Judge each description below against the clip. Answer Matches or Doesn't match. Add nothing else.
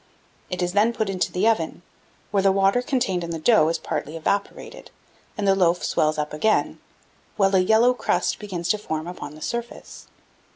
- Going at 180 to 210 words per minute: Matches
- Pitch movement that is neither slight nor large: Matches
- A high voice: Matches